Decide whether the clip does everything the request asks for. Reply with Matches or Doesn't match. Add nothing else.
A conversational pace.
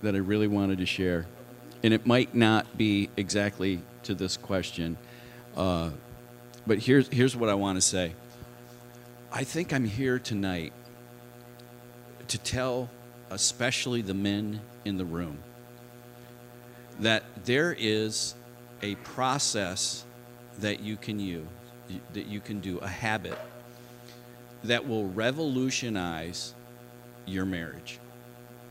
Doesn't match